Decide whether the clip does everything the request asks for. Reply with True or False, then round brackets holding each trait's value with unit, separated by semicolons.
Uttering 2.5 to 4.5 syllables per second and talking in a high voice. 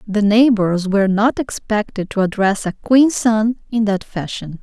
True (4.3 syllables/s; 210 Hz)